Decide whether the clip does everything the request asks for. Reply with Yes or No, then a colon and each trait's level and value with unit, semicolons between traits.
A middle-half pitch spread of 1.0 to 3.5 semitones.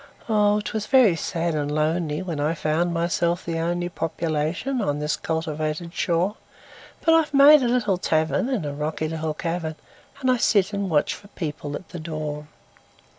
No: average, 4.6 semitones